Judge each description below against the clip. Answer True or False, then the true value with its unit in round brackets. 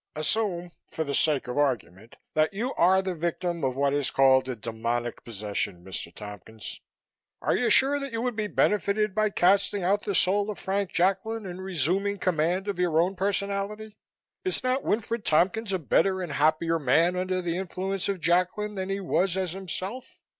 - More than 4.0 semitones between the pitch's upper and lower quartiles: True (4.6 semitones)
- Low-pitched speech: False (185 Hz)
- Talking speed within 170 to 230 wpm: True (180 wpm)